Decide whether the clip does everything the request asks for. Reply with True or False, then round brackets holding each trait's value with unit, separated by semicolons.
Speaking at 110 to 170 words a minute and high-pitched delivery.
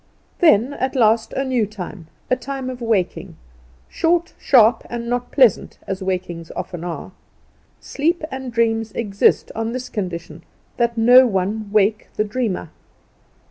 True (140 wpm; 225 Hz)